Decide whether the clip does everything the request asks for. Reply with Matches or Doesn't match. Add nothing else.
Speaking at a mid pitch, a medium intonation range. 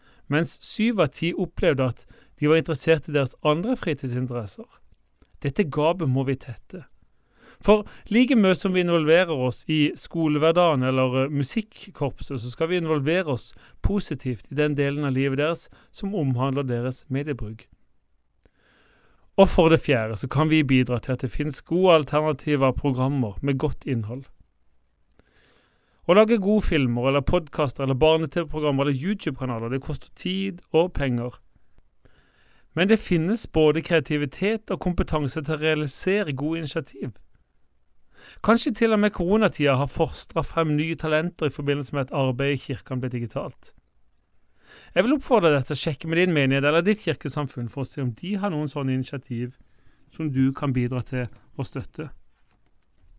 Matches